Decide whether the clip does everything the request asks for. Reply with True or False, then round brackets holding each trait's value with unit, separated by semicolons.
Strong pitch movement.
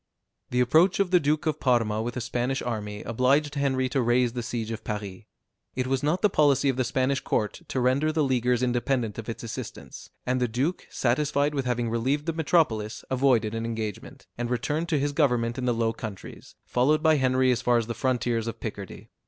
False (3.4 semitones)